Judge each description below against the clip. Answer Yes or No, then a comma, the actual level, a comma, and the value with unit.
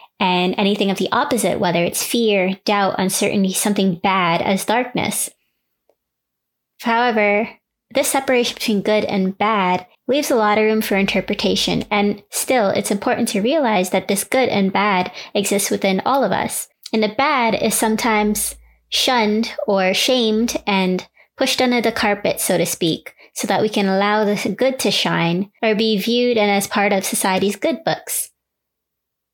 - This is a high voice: Yes, high, 210 Hz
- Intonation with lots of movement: No, average, 2.9 semitones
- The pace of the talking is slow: No, average, 160 wpm